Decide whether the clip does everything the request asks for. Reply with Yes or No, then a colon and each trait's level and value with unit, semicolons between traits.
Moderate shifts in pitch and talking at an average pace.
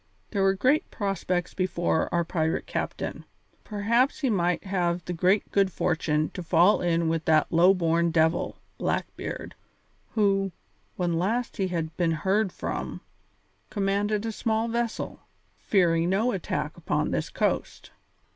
Yes: average, 3.4 semitones; average, 145 wpm